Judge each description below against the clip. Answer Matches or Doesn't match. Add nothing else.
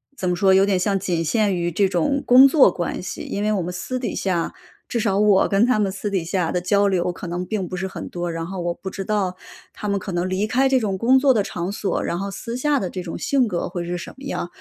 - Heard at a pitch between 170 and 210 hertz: Matches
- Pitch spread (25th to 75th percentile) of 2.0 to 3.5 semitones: Matches